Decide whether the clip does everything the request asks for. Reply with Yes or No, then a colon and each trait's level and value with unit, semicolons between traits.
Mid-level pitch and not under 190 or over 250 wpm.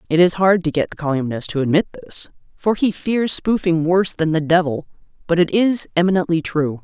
Yes: medium, 170 Hz; average, 200 wpm